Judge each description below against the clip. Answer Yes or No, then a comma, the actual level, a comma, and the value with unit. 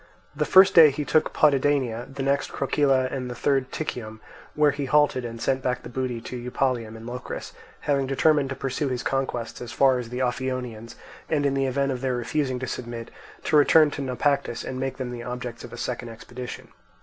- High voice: No, low, 130 Hz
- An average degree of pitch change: No, narrow, 2.2 semitones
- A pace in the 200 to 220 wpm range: Yes, fast, 205 wpm